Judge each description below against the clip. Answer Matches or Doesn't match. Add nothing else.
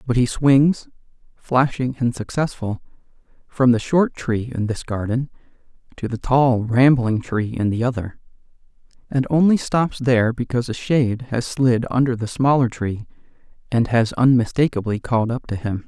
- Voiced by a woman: Doesn't match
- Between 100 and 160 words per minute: Matches